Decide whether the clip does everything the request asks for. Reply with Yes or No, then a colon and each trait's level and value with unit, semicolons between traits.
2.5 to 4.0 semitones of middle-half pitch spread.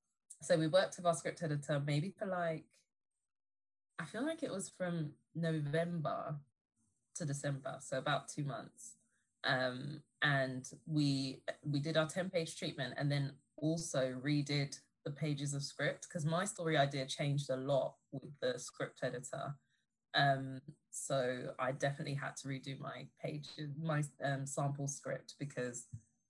Yes: average, 3.0 semitones